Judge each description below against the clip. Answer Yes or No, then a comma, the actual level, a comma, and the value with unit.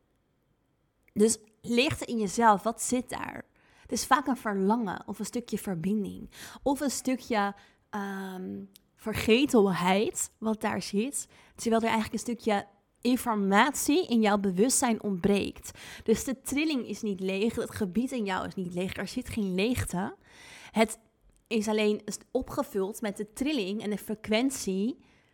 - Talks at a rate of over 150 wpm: No, average, 145 wpm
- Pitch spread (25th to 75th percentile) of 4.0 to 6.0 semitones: No, average, 2.9 semitones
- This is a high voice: Yes, high, 215 Hz